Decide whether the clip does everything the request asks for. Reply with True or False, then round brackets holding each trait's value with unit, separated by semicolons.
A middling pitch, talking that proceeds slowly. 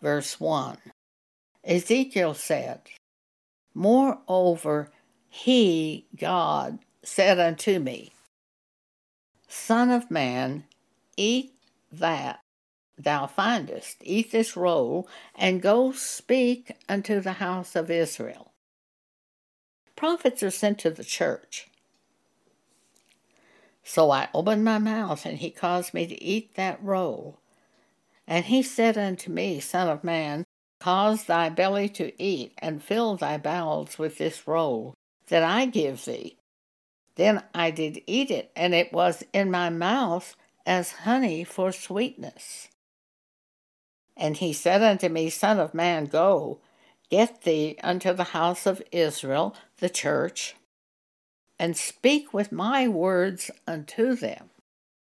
True (180 Hz; 120 wpm)